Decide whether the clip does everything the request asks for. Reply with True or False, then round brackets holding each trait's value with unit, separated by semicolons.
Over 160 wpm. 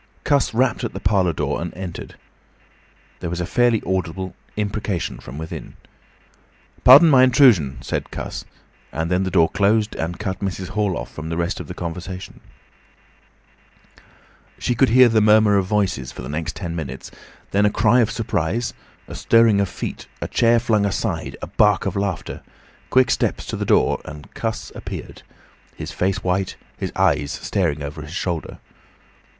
True (170 wpm)